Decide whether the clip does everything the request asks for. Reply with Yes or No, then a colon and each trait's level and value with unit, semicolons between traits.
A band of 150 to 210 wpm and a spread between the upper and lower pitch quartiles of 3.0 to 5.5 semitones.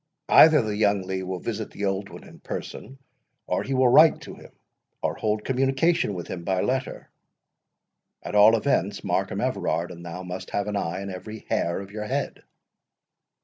Yes: average, 185 wpm; average, 4.2 semitones